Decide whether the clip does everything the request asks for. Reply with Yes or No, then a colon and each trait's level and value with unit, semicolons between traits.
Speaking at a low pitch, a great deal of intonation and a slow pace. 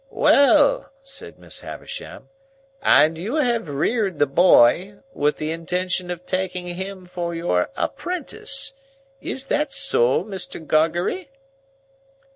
No: medium, 180 Hz; wide, 6.8 semitones; slow, 115 wpm